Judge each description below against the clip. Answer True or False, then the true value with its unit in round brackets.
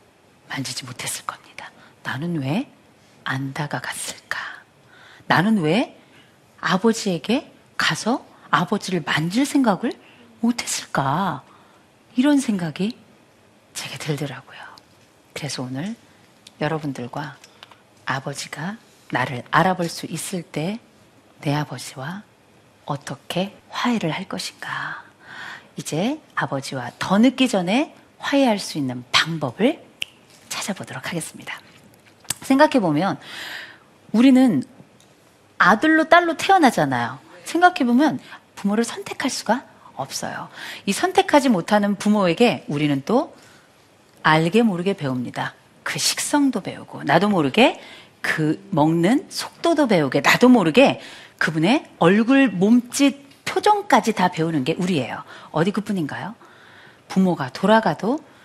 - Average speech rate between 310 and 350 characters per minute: False (245 characters per minute)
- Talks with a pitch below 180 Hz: False (185 Hz)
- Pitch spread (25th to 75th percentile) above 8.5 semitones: True (9.0 semitones)